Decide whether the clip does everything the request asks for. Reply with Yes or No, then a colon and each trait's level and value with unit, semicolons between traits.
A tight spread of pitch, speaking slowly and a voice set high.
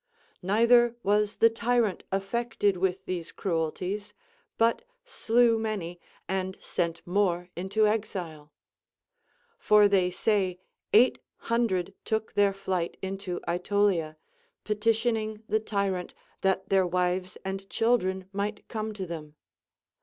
No: average, 3.1 semitones; slow, 115 wpm; high, 195 Hz